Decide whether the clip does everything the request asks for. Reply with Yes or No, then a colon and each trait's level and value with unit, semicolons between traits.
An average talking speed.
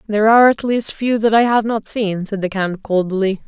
No: fast, 240 wpm